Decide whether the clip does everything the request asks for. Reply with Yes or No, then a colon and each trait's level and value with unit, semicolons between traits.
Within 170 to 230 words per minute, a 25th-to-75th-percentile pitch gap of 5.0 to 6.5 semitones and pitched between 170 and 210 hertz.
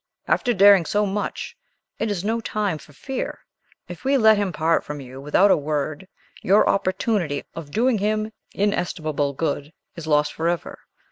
No: average, 160 wpm; wide, 5.6 semitones; medium, 185 Hz